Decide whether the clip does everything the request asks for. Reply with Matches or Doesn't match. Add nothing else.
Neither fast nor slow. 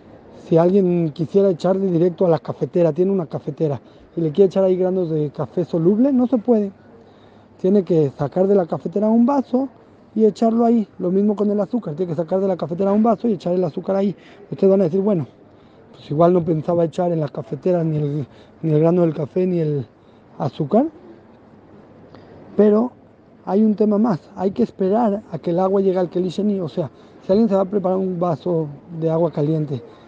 Doesn't match